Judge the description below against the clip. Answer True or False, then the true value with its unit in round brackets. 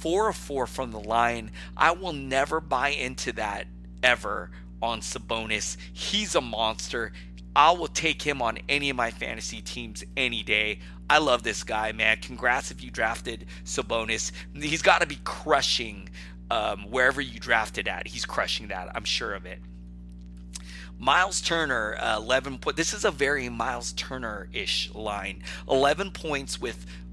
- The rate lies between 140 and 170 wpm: True (160 wpm)